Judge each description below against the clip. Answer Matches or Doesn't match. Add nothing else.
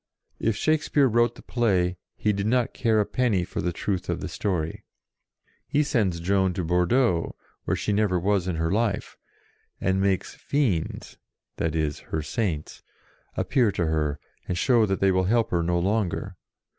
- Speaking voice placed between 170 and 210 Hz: Doesn't match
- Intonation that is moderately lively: Matches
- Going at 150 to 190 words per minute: Matches